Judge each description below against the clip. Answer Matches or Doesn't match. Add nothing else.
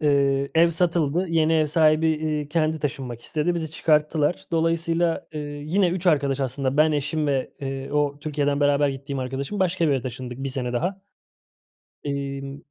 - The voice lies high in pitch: Doesn't match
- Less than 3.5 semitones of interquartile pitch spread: Matches